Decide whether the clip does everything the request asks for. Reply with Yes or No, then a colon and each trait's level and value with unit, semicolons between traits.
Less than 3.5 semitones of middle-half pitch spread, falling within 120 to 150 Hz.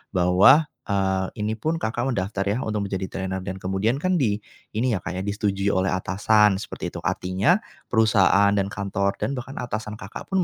No: narrow, 2.6 semitones; low, 100 Hz